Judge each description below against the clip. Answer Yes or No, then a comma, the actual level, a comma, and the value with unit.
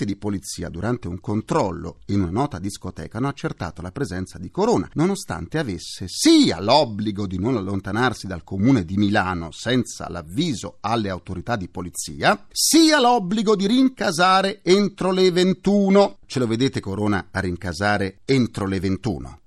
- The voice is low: Yes, low, 105 Hz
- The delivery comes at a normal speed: Yes, average, 150 wpm